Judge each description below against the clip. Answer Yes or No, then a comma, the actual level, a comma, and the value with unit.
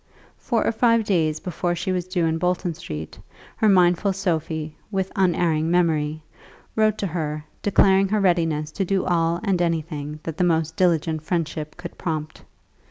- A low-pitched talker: No, medium, 170 Hz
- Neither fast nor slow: Yes, average, 165 wpm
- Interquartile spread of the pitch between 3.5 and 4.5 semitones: No, average, 3.1 semitones